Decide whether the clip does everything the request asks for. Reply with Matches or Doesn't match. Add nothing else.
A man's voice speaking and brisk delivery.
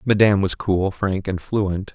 Doesn't match